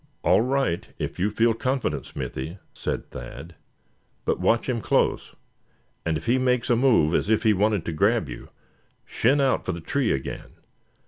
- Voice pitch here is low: Yes, low, 110 Hz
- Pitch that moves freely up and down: Yes, wide, 6.8 semitones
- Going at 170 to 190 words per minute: Yes, average, 175 wpm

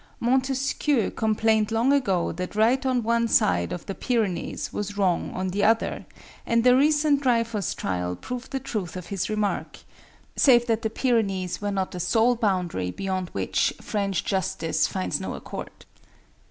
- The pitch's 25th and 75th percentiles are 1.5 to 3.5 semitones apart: No, average, 4.5 semitones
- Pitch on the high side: Yes, high, 215 Hz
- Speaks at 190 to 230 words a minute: No, average, 160 wpm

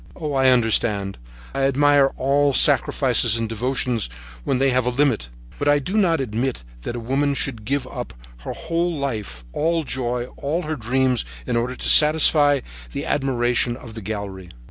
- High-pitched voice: No, low, 130 Hz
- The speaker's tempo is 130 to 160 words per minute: No, average, 170 wpm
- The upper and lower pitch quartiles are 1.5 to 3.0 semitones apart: No, average, 3.6 semitones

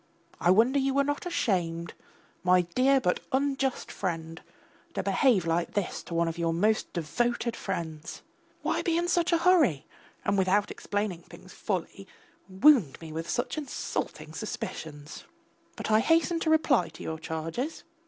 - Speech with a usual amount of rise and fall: No, wide, 8.4 semitones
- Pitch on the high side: Yes, high, 200 Hz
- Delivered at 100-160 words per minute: Yes, average, 155 wpm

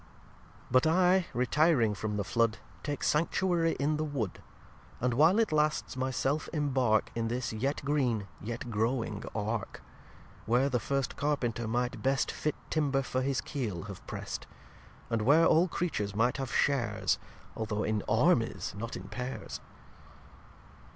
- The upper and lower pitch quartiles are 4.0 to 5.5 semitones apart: Yes, average, 4.6 semitones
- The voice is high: No, low, 130 Hz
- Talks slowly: No, average, 150 wpm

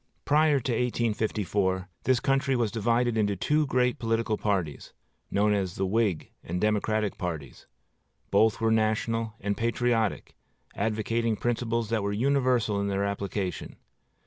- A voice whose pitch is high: No, low, 110 Hz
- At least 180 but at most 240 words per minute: No, slow, 135 wpm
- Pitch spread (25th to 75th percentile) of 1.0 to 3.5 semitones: Yes, average, 2.8 semitones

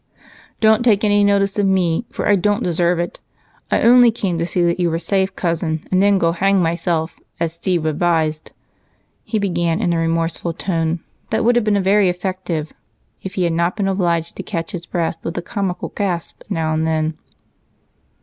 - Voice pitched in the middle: Yes, medium, 175 Hz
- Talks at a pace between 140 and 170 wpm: No, average, 190 wpm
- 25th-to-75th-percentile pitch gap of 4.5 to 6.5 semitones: No, average, 3.1 semitones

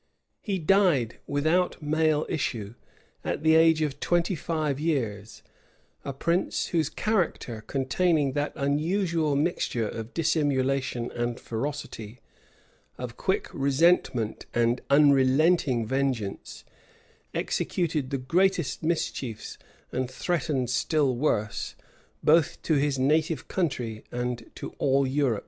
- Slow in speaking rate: Yes, slow, 110 wpm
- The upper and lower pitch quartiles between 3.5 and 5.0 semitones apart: Yes, average, 4.3 semitones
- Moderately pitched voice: Yes, medium, 145 Hz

